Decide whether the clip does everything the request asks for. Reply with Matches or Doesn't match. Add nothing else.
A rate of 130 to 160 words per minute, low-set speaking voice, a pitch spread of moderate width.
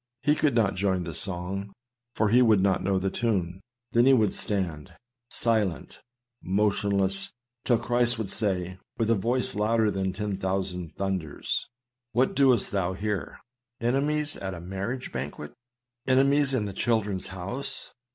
Matches